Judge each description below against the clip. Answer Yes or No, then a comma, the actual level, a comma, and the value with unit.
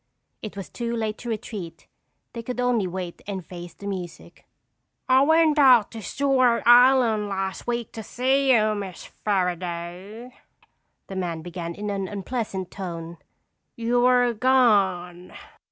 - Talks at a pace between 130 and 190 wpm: Yes, average, 140 wpm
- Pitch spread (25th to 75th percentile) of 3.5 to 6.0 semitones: Yes, average, 5.0 semitones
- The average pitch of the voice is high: Yes, high, 210 Hz